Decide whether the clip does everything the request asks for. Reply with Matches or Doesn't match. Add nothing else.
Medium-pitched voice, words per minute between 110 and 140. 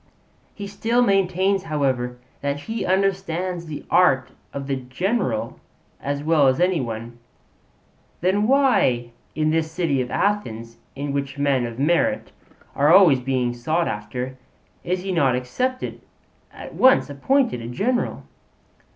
Matches